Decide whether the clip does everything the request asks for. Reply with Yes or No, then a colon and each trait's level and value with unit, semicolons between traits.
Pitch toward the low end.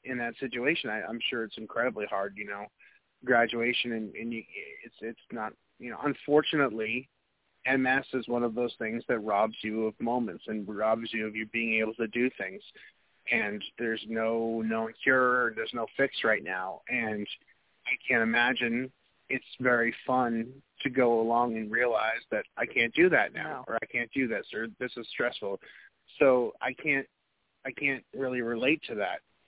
Yes: low, 120 Hz